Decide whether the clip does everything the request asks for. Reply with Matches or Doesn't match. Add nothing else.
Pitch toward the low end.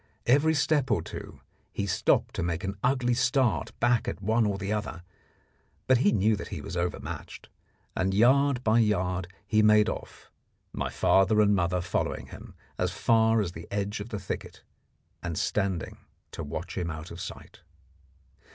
Matches